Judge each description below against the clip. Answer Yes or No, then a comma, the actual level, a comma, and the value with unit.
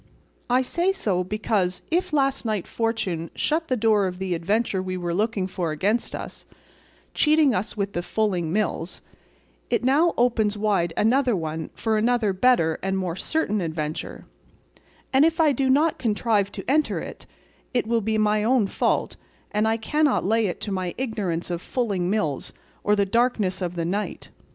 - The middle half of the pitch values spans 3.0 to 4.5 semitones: No, average, 5.0 semitones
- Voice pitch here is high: Yes, high, 210 Hz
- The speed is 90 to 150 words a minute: No, average, 175 wpm